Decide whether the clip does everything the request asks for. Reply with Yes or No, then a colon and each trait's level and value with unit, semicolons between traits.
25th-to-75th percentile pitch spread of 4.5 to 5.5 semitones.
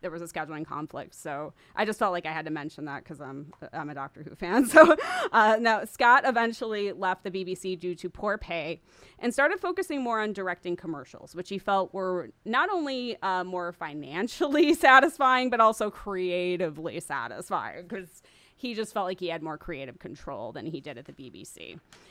Yes: average, 5.2 semitones